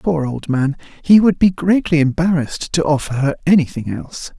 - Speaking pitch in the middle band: Yes, medium, 155 Hz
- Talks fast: No, average, 180 wpm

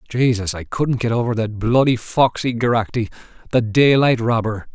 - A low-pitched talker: Yes, low, 115 Hz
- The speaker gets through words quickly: No, average, 150 wpm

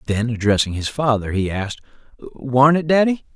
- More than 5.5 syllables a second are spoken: No, 5.3 syllables/s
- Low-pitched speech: Yes, low, 125 Hz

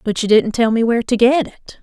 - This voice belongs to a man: No, female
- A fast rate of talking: Yes, fast, 295 wpm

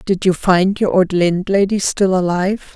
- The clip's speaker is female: Yes, female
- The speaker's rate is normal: Yes, average, 175 wpm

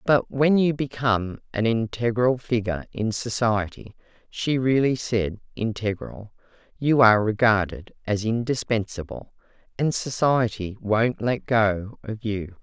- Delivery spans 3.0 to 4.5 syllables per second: Yes, 4.4 syllables/s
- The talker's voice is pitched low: Yes, low, 115 Hz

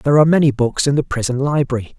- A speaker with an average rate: No, fast, 240 wpm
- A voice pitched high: No, low, 135 Hz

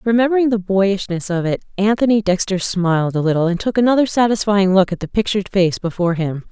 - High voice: Yes, high, 195 Hz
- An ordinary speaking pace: Yes, average, 195 wpm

